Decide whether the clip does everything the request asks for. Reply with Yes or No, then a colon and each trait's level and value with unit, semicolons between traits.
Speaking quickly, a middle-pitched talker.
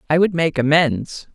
No: average, 180 wpm; medium, 155 Hz